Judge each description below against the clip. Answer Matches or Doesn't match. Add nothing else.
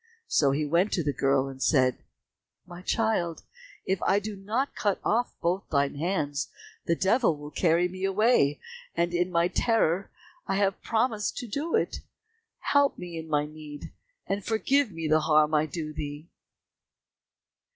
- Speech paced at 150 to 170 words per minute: Matches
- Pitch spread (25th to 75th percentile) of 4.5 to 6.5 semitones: Matches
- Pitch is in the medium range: Matches